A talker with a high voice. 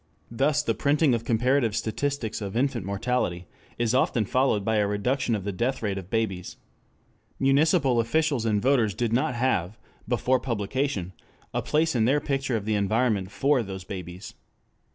No: low, 115 Hz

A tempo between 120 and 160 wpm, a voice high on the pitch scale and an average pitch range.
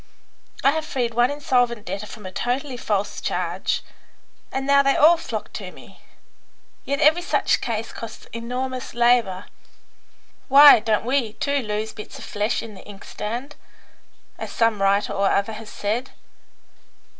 Yes: average, 150 wpm; high, 235 Hz; average, 4.2 semitones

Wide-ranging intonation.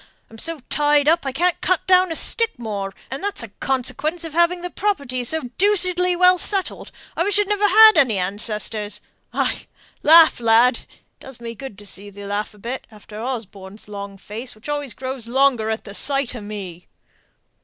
Yes: wide, 8.2 semitones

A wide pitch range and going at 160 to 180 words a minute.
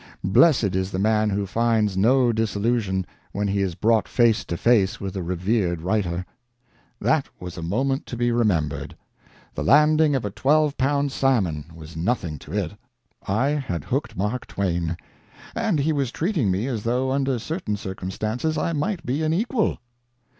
Yes: wide, 6.2 semitones; average, 170 wpm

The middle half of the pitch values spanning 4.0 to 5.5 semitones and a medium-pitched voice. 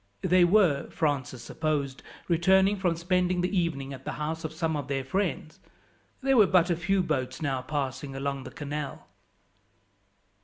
Yes: average, 4.6 semitones; medium, 160 Hz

